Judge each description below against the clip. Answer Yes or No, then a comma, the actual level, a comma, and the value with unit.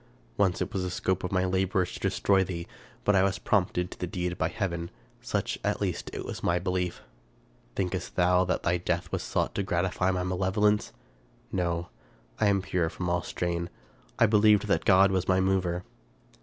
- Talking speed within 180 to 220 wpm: Yes, average, 185 wpm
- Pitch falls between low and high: No, very low, 90 Hz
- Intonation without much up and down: Yes, narrow, 1.5 semitones